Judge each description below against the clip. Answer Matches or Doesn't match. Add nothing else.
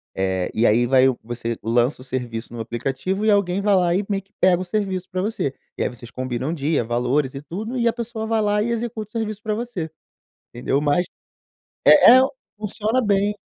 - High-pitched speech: Doesn't match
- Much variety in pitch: Matches